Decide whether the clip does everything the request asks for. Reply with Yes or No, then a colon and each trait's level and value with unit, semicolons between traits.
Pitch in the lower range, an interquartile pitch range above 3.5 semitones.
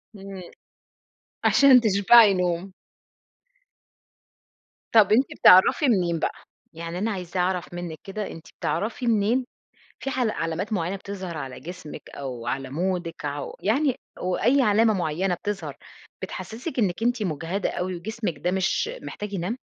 No: high, 190 Hz; average, 4.2 semitones